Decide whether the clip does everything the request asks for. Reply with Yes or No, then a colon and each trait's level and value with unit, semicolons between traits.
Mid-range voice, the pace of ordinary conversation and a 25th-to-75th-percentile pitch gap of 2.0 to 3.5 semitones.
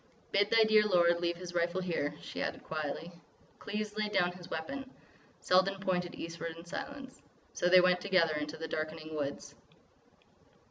Yes: medium, 175 Hz; average, 165 wpm; average, 3.2 semitones